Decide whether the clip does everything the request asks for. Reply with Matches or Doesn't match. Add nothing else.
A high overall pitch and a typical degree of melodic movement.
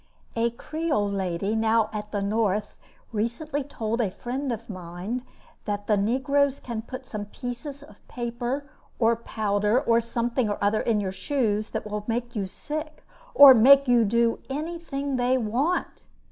Matches